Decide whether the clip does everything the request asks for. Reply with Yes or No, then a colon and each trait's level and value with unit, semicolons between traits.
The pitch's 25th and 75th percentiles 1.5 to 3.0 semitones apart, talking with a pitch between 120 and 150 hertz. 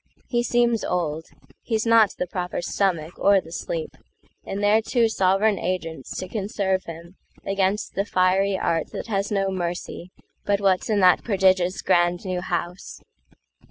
No: narrow, 2.5 semitones; high, 190 Hz